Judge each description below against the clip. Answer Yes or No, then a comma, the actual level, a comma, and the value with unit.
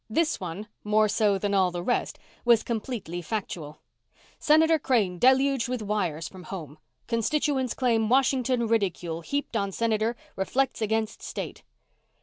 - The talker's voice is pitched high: Yes, high, 220 Hz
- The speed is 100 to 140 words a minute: Yes, slow, 135 wpm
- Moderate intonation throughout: Yes, average, 4.8 semitones